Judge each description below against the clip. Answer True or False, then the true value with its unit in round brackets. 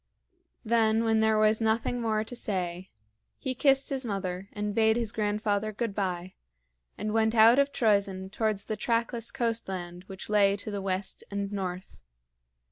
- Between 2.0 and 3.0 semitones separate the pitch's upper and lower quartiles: True (2.5 semitones)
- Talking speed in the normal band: True (160 wpm)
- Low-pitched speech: False (215 Hz)